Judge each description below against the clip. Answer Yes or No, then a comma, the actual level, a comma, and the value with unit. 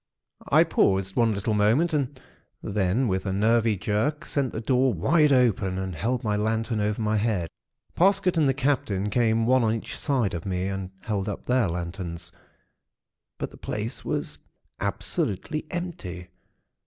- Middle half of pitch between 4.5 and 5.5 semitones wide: Yes, average, 5.0 semitones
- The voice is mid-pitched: No, low, 110 Hz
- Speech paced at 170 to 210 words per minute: No, average, 160 wpm